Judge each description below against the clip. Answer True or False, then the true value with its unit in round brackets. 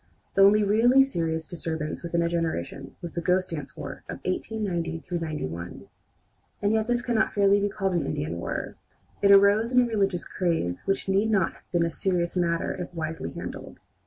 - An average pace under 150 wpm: False (185 wpm)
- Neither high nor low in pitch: True (180 Hz)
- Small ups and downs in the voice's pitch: False (3.7 semitones)